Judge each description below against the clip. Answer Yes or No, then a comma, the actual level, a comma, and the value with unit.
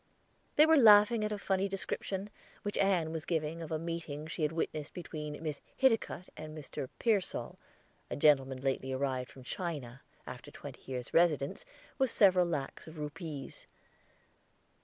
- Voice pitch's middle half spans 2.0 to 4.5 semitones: No, average, 4.9 semitones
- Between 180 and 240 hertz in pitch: No, medium, 160 Hz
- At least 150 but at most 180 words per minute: Yes, average, 160 wpm